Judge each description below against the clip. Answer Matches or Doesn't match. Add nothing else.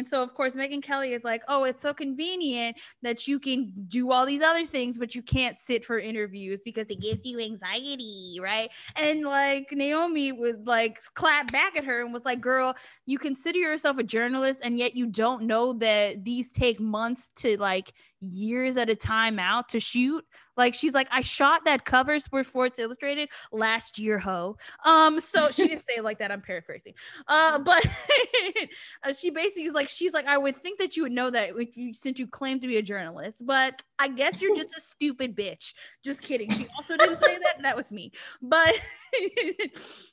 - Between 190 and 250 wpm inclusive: Matches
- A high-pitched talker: Matches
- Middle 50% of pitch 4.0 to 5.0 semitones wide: Matches